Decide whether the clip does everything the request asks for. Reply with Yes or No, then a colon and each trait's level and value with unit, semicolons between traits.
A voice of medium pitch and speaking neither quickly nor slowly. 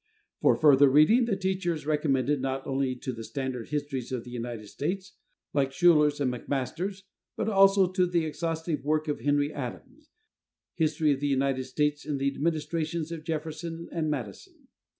Yes: medium, 150 Hz; average, 170 wpm